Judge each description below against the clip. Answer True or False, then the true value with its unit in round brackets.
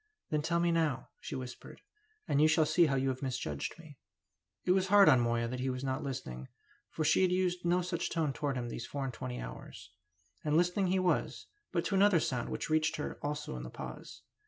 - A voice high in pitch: False (150 Hz)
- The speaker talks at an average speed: False (225 wpm)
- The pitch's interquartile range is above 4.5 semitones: True (5.3 semitones)